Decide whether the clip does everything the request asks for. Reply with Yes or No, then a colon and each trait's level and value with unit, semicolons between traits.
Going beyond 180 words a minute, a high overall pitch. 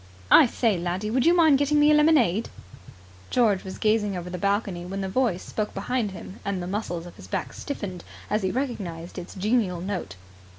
Yes: average, 200 wpm; high, 200 Hz